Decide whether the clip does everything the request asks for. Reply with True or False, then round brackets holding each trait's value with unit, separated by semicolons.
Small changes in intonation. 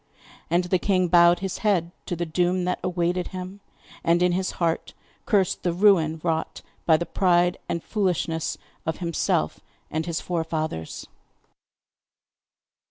True (1.8 semitones)